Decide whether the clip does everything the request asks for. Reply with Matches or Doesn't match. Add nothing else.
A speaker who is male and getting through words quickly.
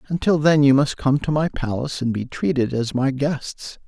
Matches